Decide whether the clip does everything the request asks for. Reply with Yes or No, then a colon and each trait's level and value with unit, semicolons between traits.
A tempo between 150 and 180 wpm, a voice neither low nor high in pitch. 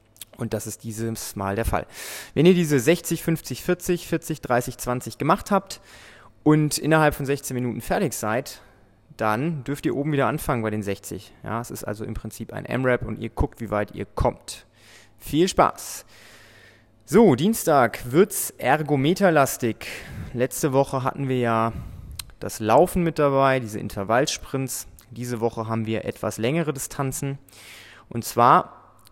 No: average, 155 wpm; low, 125 Hz